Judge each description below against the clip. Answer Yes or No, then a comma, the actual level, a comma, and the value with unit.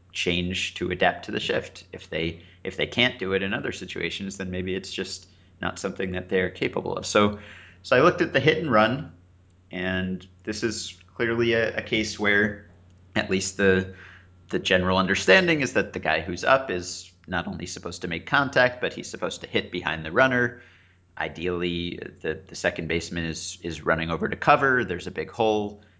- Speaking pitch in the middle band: No, very low, 95 Hz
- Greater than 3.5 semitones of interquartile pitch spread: No, narrow, 2.5 semitones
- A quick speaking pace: No, average, 195 wpm